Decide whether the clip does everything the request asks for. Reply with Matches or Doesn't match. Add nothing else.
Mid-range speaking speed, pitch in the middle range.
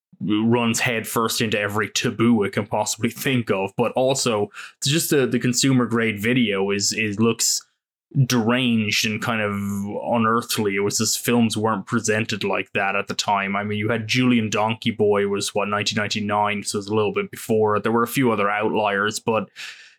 Doesn't match